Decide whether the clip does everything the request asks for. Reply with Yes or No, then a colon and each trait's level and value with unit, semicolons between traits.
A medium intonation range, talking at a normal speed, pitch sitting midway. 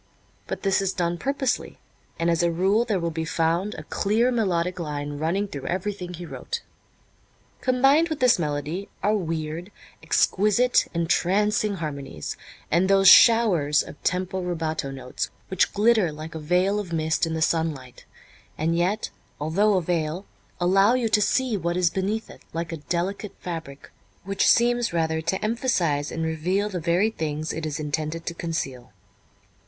Yes: average, 4.2 semitones; average, 160 wpm; medium, 175 Hz